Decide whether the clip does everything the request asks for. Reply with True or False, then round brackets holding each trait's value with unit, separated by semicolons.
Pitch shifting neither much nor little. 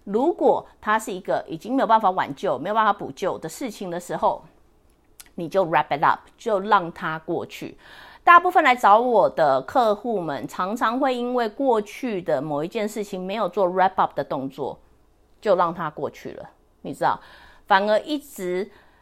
True (4.8 semitones)